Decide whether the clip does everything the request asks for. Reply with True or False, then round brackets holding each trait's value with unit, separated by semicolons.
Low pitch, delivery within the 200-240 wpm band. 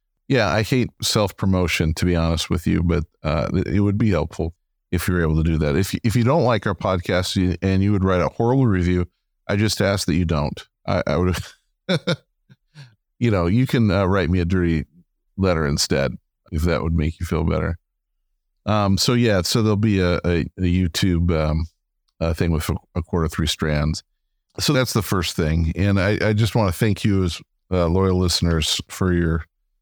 True (90 Hz; 205 wpm)